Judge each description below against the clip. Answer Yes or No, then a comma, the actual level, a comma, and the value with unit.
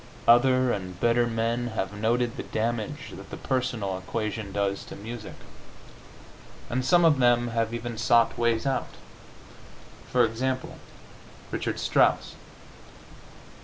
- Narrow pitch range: Yes, narrow, 2.0 semitones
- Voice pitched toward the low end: Yes, low, 120 Hz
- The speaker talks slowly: Yes, slow, 125 wpm